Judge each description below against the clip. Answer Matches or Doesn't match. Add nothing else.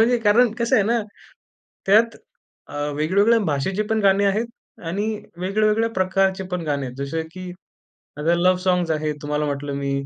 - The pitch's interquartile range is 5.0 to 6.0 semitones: Matches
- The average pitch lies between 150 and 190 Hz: Matches